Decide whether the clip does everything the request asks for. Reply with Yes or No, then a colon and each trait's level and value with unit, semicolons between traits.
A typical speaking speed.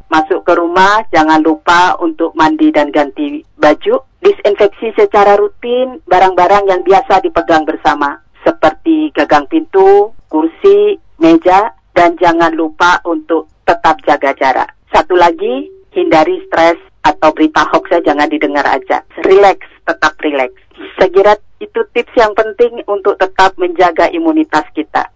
Yes: average, 125 wpm